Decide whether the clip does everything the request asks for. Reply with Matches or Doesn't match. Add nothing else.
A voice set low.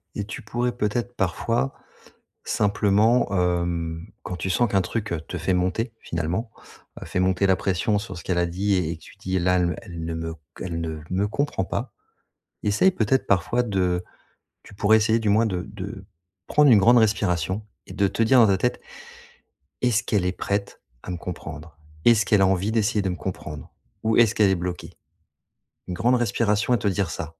Matches